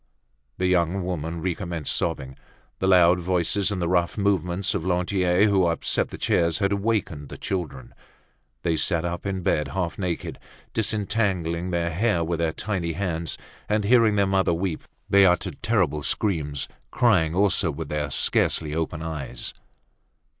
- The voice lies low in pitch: Yes, very low, 90 Hz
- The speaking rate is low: No, average, 155 wpm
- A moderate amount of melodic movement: Yes, average, 3.0 semitones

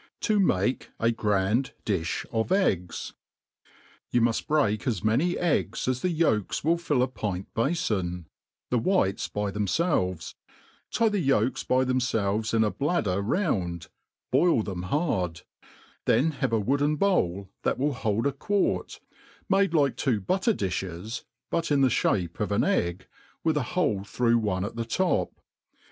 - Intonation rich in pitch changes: Yes, wide, 7.4 semitones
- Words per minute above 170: No, average, 155 wpm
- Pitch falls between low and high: No, low, 115 Hz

